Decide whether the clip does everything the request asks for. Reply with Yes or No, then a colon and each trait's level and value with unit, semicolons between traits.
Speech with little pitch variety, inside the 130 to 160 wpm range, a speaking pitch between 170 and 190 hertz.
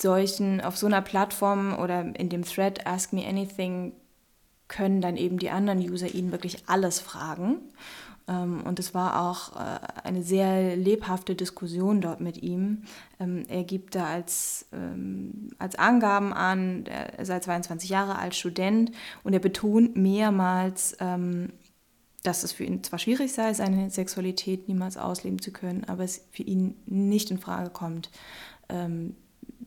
Yes: narrow, 1.8 semitones; average, 145 wpm; medium, 185 Hz